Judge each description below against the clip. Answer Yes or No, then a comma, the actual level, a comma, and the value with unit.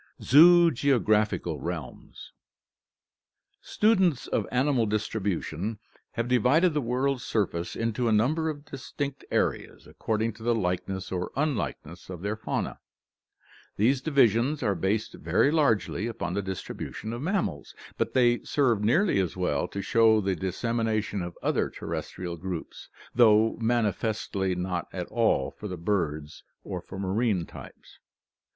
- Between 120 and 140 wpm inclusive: Yes, slow, 135 wpm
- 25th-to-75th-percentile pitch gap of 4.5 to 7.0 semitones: Yes, average, 5.0 semitones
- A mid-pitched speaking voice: No, low, 110 Hz